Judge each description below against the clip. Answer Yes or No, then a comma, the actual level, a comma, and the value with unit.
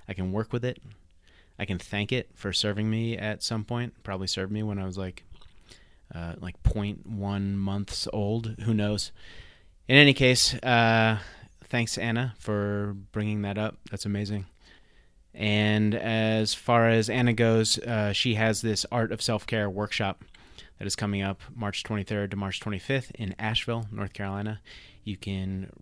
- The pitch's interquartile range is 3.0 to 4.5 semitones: No, narrow, 2.4 semitones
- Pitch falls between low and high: No, low, 105 Hz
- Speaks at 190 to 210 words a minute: No, average, 165 wpm